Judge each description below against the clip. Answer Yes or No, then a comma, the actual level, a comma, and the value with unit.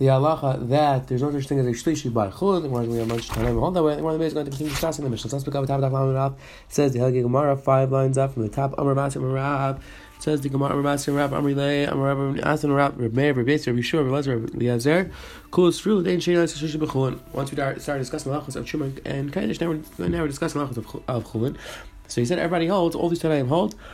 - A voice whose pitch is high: No, medium, 140 Hz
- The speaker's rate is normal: Yes, average, 165 wpm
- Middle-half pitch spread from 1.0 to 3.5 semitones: Yes, narrow, 2.5 semitones